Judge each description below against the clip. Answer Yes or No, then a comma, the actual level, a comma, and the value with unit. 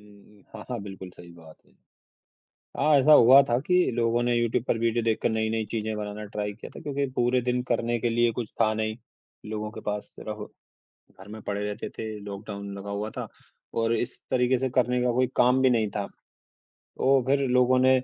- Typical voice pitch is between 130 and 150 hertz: No, low, 115 Hz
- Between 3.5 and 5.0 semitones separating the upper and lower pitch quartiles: No, average, 2.9 semitones